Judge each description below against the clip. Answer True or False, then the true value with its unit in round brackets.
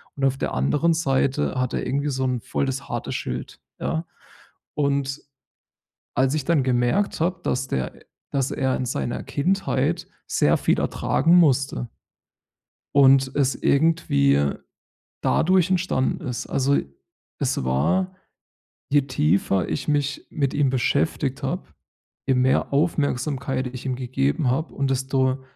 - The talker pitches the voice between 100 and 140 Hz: True (135 Hz)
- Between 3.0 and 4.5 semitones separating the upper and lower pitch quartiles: False (2.4 semitones)